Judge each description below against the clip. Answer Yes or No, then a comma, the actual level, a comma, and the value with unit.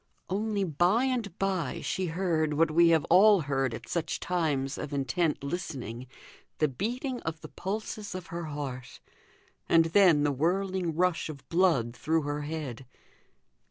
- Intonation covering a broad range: No, average, 4.5 semitones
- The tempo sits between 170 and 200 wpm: No, average, 155 wpm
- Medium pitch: Yes, medium, 165 Hz